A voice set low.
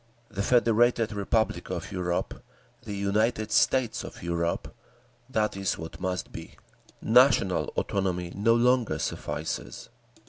Yes: low, 105 Hz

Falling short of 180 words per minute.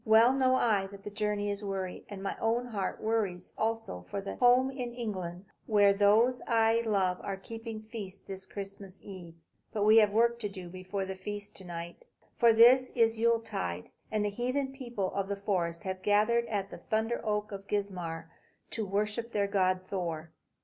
No: average, 190 wpm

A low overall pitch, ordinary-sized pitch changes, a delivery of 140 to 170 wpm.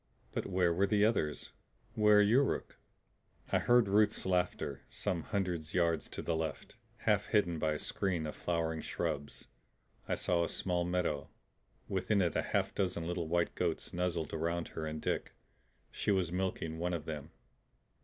Yes: very low, 85 Hz; average, 3.0 semitones; average, 165 wpm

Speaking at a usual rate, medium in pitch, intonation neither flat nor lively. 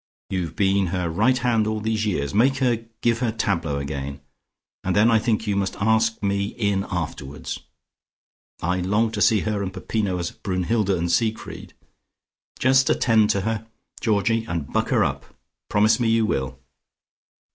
No: average, 165 wpm; low, 105 Hz; average, 3.5 semitones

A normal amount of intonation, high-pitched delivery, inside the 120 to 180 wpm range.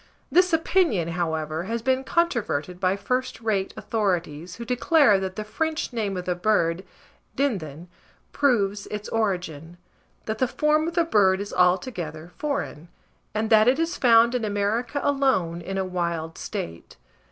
No: wide, 6.2 semitones; high, 205 Hz; average, 150 wpm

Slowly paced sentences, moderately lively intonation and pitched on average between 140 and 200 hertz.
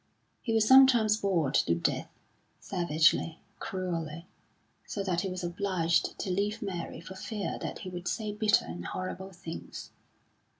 No: average, 145 wpm; average, 3.7 semitones; medium, 185 Hz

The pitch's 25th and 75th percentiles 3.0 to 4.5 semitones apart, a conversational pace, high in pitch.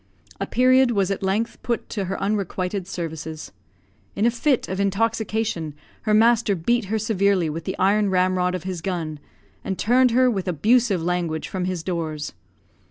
Yes: average, 3.8 semitones; average, 165 wpm; high, 195 Hz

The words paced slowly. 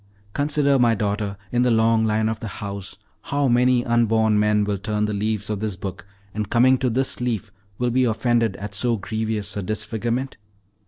No: average, 190 wpm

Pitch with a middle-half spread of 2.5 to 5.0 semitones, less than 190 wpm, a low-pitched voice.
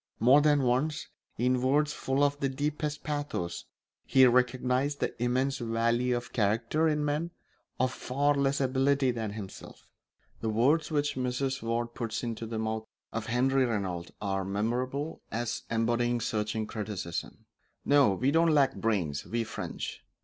Yes: average, 3.8 semitones; average, 150 wpm; low, 125 Hz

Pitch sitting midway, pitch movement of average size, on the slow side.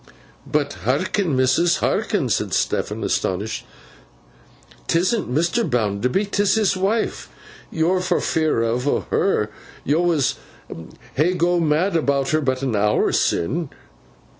No: medium, 155 Hz; wide, 5.9 semitones; slow, 120 wpm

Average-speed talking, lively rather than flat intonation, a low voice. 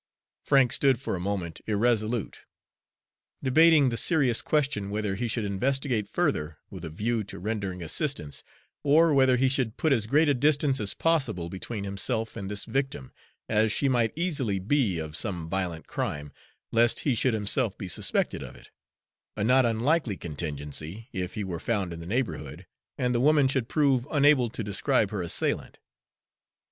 Yes: average, 170 wpm; wide, 5.7 semitones; low, 115 Hz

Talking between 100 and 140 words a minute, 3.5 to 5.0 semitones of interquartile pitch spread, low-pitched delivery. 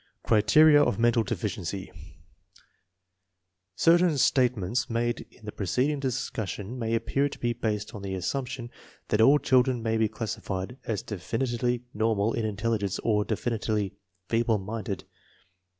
No: slow, 135 wpm; average, 2.9 semitones; low, 115 Hz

